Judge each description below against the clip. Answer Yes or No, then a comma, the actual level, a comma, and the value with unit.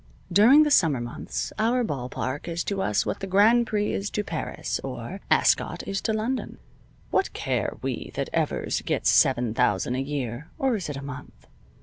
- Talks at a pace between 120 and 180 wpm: No, average, 190 wpm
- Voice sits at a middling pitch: Yes, medium, 175 Hz